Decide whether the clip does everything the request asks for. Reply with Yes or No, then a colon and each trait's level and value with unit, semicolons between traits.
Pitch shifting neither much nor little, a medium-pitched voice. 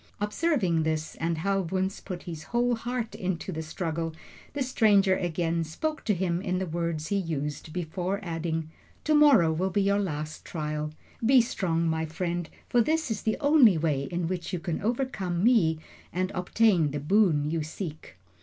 Yes: average, 4.4 semitones; medium, 180 Hz